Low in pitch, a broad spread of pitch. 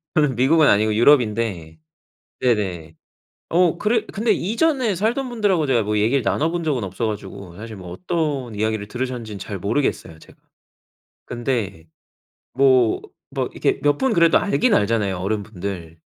Yes: low, 115 Hz; wide, 8.2 semitones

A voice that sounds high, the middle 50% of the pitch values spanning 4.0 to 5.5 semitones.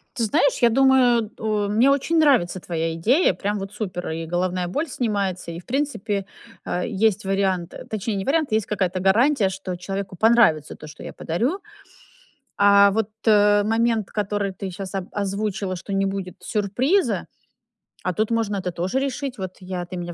No: high, 200 Hz; average, 3.6 semitones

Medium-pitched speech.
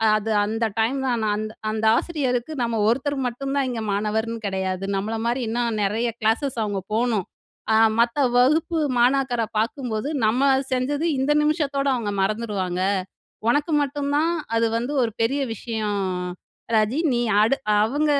No: high, 235 Hz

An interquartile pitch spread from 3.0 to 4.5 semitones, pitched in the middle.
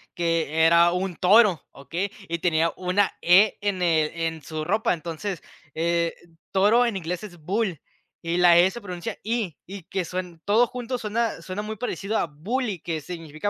Yes: average, 3.6 semitones; medium, 180 Hz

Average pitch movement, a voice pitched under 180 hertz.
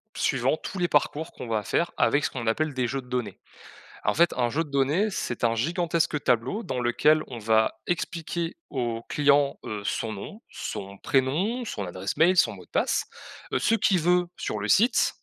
No: wide, 6.7 semitones; medium, 140 Hz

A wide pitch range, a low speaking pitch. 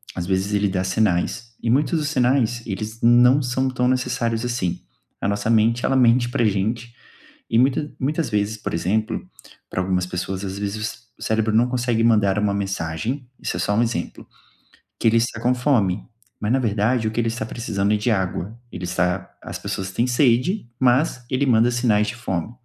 No: average, 3.4 semitones; low, 115 Hz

